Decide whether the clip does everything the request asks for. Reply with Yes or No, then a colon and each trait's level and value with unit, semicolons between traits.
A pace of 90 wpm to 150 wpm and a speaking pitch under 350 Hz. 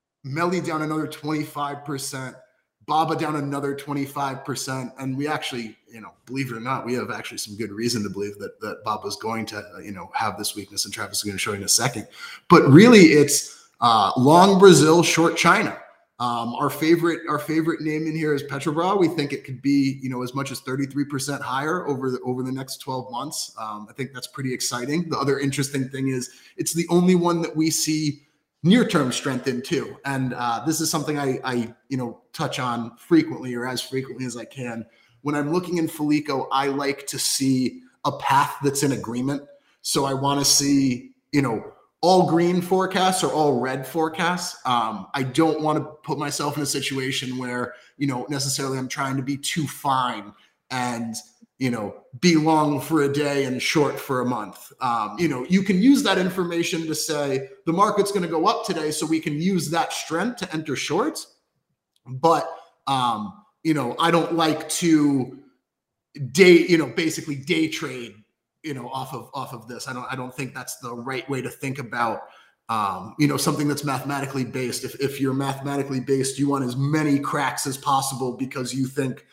No: fast, 205 wpm; medium, 140 Hz